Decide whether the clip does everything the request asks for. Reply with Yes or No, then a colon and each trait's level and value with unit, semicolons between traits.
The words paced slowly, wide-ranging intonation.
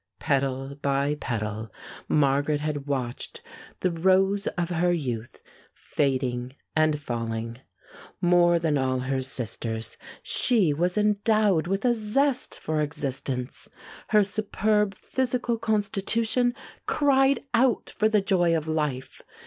Yes: slow, 115 wpm; wide, 7.6 semitones